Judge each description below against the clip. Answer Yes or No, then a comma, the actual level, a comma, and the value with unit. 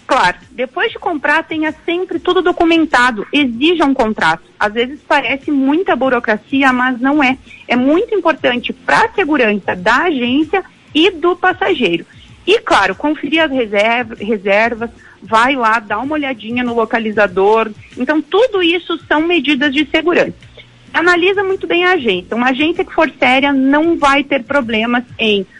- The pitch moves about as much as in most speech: No, wide, 6.0 semitones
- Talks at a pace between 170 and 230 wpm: No, average, 150 wpm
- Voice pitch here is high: Yes, very high, 285 Hz